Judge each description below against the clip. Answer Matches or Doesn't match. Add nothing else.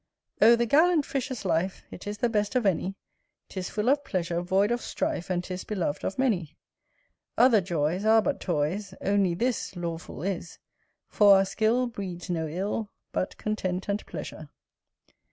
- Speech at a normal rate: Matches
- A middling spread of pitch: Matches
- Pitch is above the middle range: Matches